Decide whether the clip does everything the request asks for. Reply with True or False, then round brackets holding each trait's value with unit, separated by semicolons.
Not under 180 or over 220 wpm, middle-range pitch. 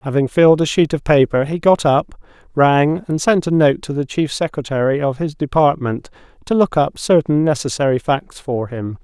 True (195 wpm; 145 Hz)